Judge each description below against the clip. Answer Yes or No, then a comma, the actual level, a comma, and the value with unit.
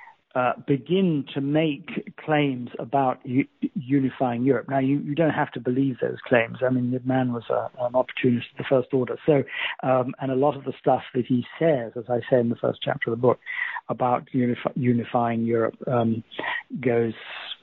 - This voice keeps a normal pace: Yes, average, 195 wpm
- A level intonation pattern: No, average, 3.0 semitones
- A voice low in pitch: Yes, low, 130 Hz